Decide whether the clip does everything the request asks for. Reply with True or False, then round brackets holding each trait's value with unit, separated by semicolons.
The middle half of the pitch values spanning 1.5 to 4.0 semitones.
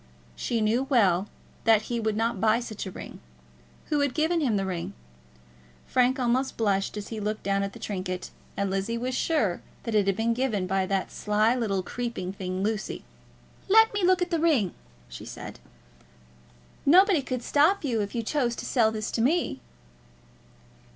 False (4.8 semitones)